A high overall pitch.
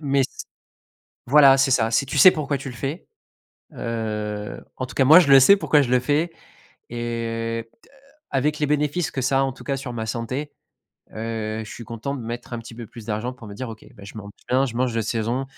No: low, 125 Hz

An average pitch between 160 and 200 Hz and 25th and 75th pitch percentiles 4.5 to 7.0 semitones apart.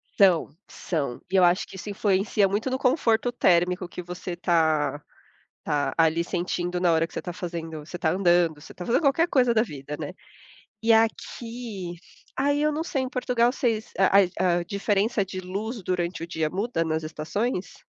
Yes: medium, 185 Hz; average, 4.9 semitones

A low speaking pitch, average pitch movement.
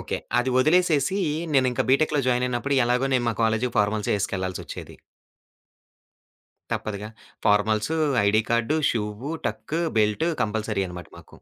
Yes: low, 115 Hz; average, 4.2 semitones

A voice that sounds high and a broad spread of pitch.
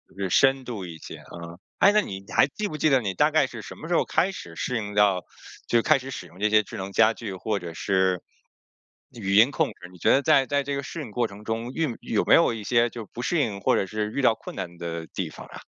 No: low, 110 Hz; wide, 5.8 semitones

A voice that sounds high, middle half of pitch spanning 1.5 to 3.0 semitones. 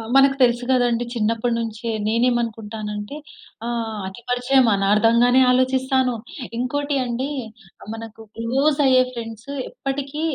Yes: high, 240 Hz; narrow, 2.5 semitones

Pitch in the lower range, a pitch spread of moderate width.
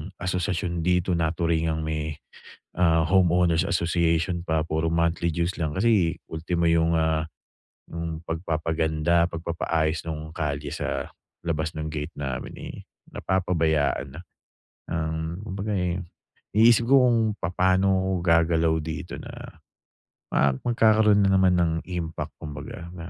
No: very low, 85 Hz; narrow, 2.1 semitones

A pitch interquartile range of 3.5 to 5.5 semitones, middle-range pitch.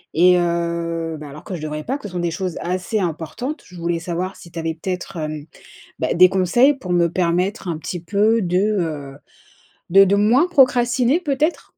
Yes: average, 4.0 semitones; medium, 180 Hz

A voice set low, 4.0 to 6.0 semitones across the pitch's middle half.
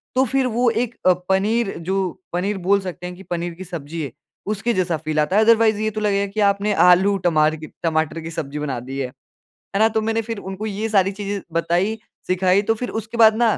No: high, 195 Hz; average, 4.4 semitones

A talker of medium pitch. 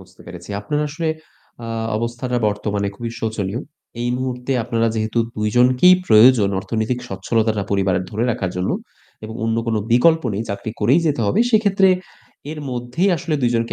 No: low, 115 Hz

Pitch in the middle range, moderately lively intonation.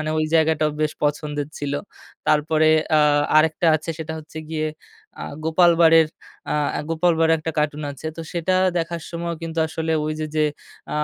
No: medium, 160 Hz; narrow, 1.1 semitones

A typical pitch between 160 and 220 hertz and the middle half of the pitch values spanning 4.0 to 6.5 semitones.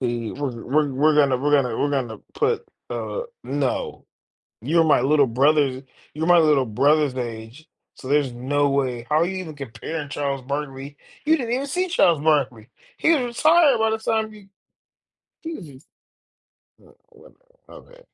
No: medium, 145 Hz; average, 5.0 semitones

